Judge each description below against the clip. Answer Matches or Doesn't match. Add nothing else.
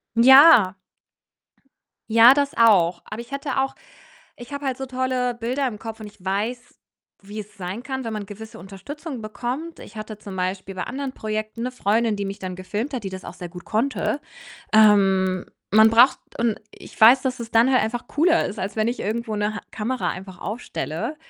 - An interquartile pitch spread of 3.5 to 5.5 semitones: Matches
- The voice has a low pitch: Doesn't match